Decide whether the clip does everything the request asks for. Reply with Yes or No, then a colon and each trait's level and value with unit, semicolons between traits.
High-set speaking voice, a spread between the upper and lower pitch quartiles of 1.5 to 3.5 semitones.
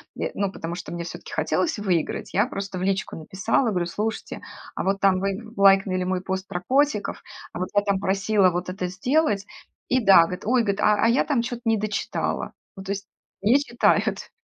Yes: high, 195 Hz; average, 2.8 semitones